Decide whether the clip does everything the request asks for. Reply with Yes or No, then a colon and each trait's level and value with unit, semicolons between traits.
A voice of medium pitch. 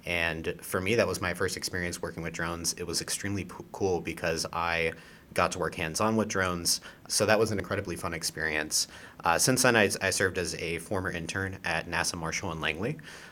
No: very low, 85 Hz